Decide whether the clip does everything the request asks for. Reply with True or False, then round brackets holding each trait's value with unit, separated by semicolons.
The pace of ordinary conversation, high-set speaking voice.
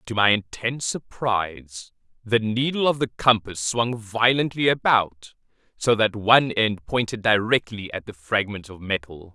False (150 wpm; 110 Hz)